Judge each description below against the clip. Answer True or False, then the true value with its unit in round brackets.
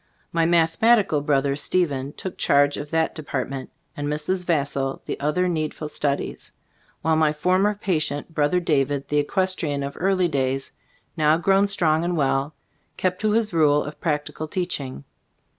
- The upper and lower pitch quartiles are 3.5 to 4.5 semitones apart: True (3.9 semitones)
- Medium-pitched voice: True (155 Hz)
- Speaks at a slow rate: False (155 wpm)